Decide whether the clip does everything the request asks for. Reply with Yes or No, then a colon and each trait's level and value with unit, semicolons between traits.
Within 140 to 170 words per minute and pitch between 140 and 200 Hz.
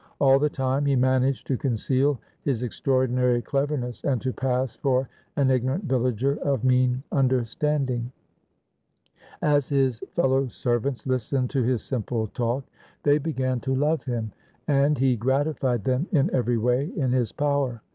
No: average, 150 wpm; low, 130 Hz